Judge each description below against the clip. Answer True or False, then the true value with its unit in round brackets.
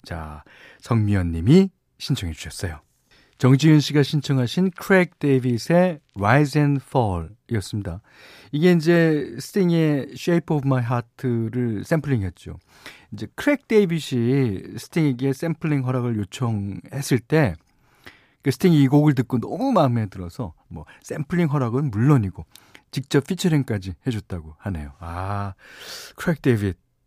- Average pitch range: False (7.0 semitones)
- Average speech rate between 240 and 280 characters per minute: False (315 characters per minute)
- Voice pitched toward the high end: False (130 Hz)